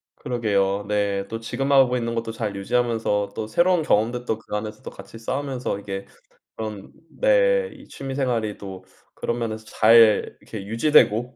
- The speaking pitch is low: Yes, low, 115 Hz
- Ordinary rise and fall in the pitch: Yes, average, 3.2 semitones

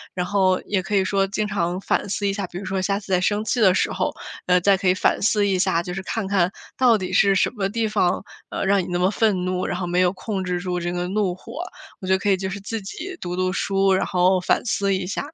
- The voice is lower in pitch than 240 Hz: Yes, high, 190 Hz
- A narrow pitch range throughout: Yes, narrow, 1.8 semitones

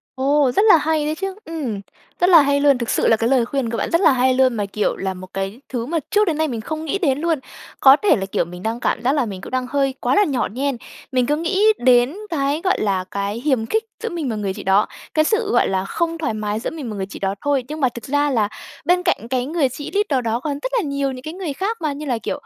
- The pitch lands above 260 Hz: Yes, very high, 270 Hz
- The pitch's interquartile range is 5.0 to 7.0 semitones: Yes, average, 5.3 semitones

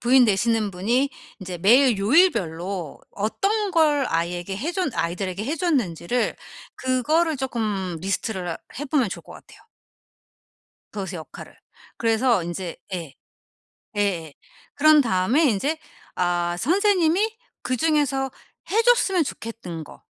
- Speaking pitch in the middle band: No, high, 230 Hz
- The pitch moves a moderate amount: No, wide, 8.4 semitones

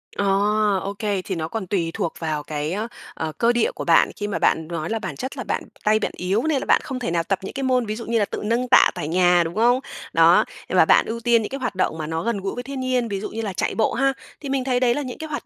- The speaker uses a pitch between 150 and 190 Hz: No, high, 220 Hz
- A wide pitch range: Yes, wide, 5.7 semitones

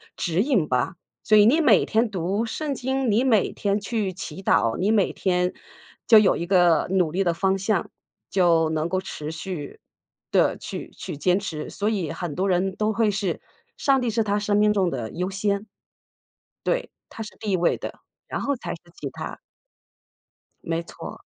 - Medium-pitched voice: No, high, 195 Hz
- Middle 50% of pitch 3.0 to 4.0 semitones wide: Yes, average, 3.7 semitones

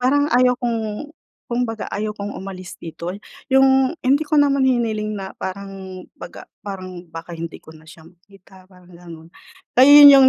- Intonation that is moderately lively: No, wide, 5.8 semitones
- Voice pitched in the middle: No, high, 200 Hz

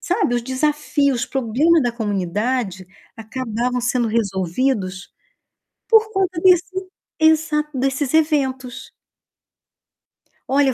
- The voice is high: Yes, very high, 260 Hz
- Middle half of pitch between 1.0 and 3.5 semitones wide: No, average, 4.8 semitones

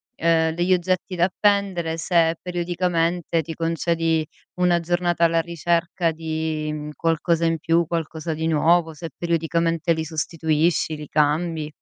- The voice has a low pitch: No, medium, 165 Hz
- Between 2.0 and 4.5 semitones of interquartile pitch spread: No, narrow, 1.3 semitones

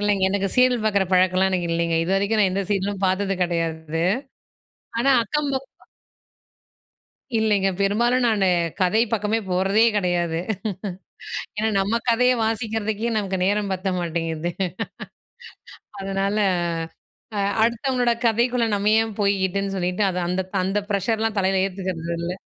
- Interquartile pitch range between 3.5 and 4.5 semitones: No, average, 3.0 semitones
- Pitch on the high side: Yes, high, 200 Hz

